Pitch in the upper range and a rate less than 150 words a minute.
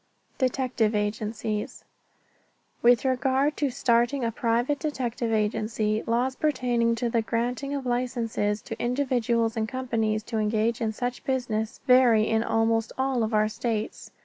Yes: high, 235 Hz; average, 140 wpm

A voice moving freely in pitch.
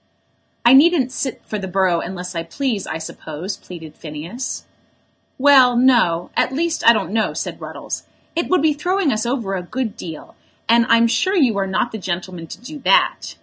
Yes: wide, 6.8 semitones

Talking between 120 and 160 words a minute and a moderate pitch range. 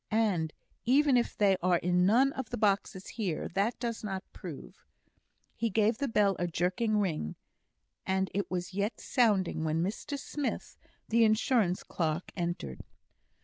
Yes: average, 155 wpm; average, 4.2 semitones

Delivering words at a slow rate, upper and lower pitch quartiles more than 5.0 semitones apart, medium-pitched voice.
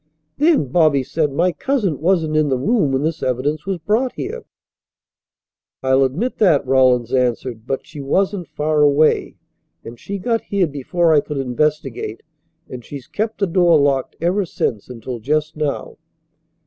No: average, 160 wpm; wide, 5.5 semitones; medium, 150 Hz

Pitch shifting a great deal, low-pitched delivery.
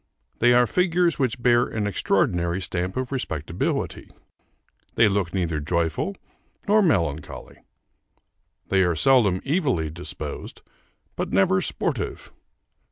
Yes: wide, 7.0 semitones; low, 100 Hz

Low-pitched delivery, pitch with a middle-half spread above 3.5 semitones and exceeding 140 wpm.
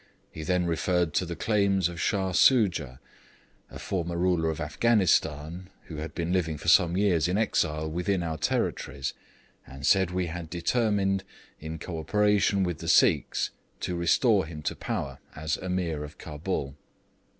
No: very low, 85 Hz; average, 3.2 semitones; average, 160 wpm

